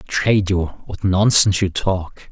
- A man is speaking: Yes, male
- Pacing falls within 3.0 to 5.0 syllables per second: Yes, 4.0 syllables/s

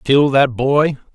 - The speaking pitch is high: No, low, 135 Hz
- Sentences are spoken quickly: No, average, 155 wpm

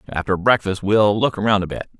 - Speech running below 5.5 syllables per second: No, 5.7 syllables/s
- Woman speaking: No, male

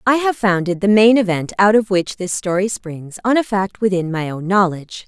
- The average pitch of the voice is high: Yes, high, 195 Hz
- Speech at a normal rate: No, fast, 225 wpm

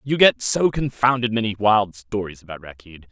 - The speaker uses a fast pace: No, average, 175 wpm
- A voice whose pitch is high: No, low, 110 Hz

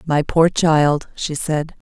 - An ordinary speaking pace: Yes, average, 155 wpm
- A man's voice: No, female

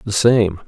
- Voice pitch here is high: No, low, 105 Hz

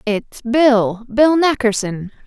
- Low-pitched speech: No, high, 240 Hz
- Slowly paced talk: Yes, slow, 80 wpm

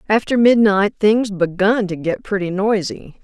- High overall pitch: Yes, high, 205 Hz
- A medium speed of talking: Yes, average, 150 wpm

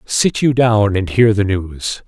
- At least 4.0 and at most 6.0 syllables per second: No, 3.6 syllables/s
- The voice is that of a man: Yes, male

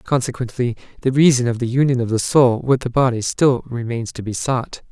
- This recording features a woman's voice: No, male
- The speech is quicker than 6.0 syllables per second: No, 5.4 syllables/s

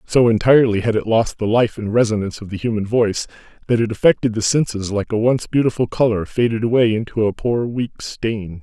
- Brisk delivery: Yes, fast, 210 wpm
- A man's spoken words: Yes, male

